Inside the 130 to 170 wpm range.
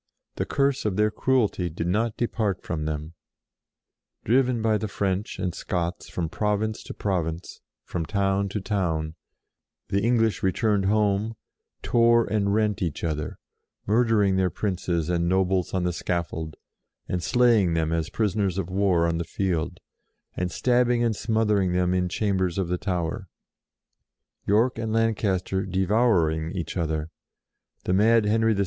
Yes: average, 160 wpm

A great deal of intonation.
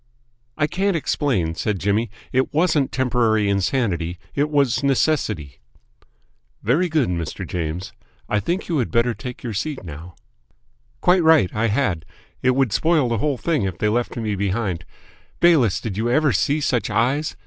Yes: wide, 6.6 semitones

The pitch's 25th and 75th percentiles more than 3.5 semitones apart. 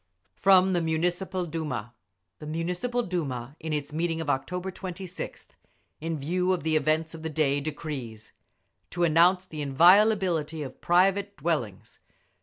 No: average, 3.1 semitones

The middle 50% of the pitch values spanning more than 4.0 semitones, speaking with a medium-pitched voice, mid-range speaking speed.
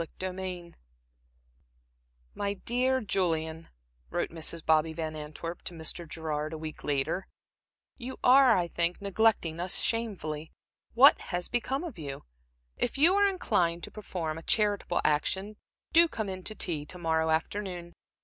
Yes: average, 5.1 semitones; medium, 175 Hz; average, 150 wpm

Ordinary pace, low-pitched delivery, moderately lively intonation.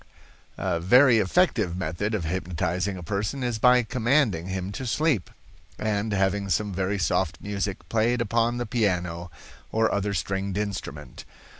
Yes: average, 145 wpm; low, 100 Hz; average, 3.9 semitones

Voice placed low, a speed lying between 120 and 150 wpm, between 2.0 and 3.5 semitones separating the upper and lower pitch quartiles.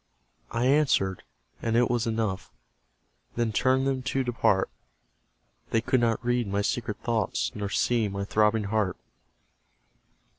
Yes: low, 115 Hz; slow, 135 wpm; average, 3.1 semitones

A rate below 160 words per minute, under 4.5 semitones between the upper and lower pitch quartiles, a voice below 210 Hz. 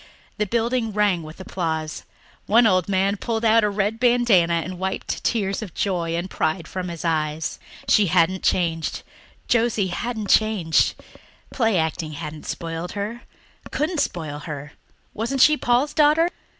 No: average, 150 wpm; average, 5.2 semitones; high, 190 Hz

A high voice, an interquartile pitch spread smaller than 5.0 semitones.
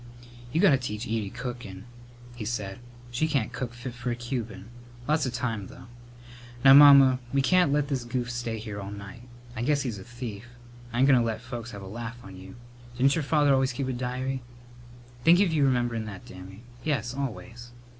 No: low, 120 Hz; average, 3.3 semitones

